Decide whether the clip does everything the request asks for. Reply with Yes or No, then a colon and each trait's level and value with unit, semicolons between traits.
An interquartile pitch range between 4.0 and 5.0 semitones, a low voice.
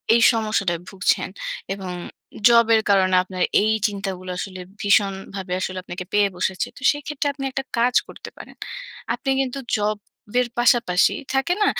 No: average, 4.3 semitones; high, 205 Hz